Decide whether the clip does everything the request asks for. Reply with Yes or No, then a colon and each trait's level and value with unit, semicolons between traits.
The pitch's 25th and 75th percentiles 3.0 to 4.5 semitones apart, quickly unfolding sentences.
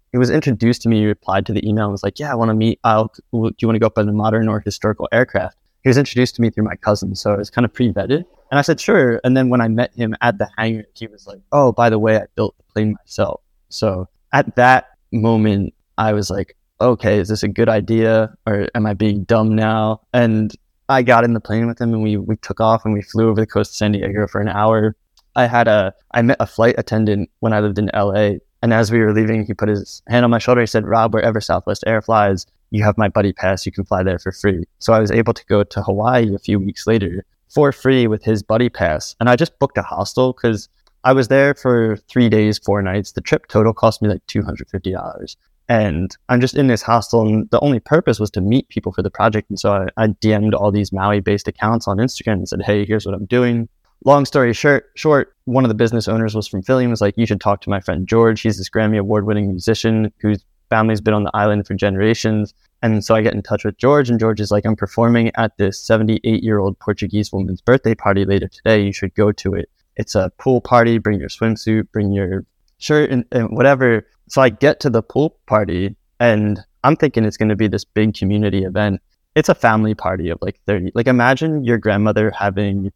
No: narrow, 2.4 semitones; fast, 245 wpm